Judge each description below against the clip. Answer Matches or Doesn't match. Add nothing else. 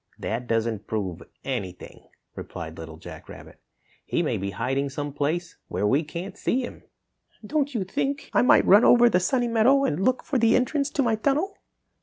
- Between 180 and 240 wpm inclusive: Matches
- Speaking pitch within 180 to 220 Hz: Matches